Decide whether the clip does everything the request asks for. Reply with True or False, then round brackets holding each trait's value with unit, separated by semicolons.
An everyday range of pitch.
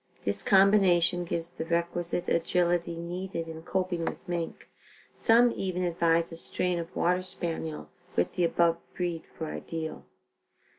False (1.4 semitones)